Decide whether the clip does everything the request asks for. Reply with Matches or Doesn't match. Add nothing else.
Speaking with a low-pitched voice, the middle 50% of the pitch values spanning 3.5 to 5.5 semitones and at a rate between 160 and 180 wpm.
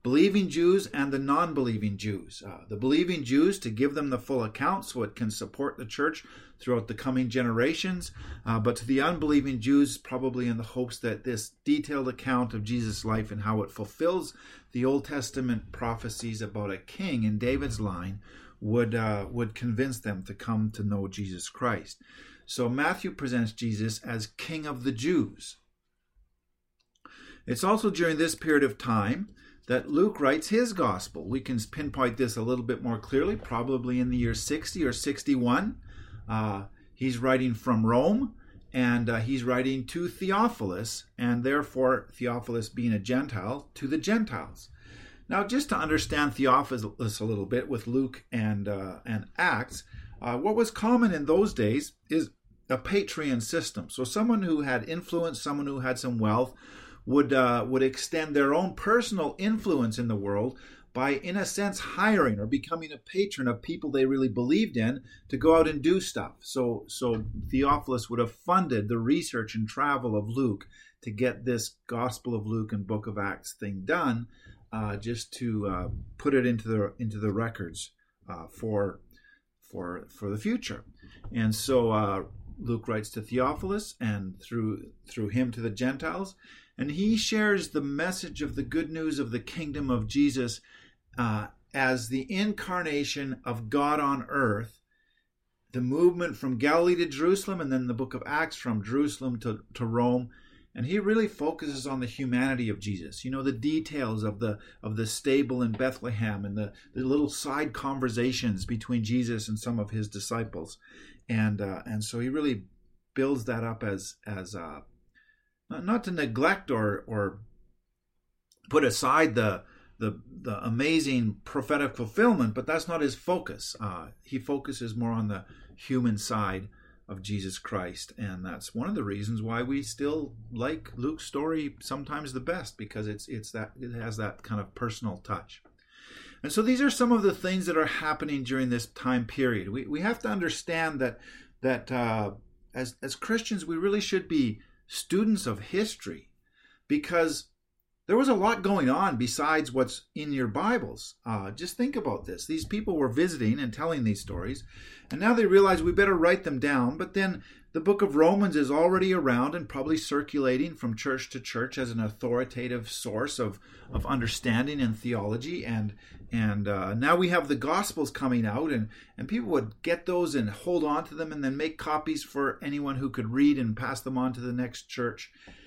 Matches